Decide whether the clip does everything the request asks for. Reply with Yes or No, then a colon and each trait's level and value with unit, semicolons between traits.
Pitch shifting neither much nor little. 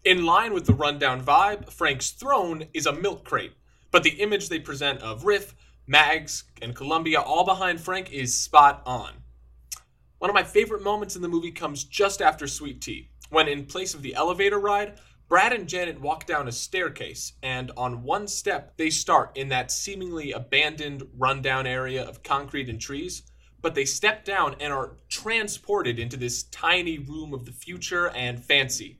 No: wide, 6.0 semitones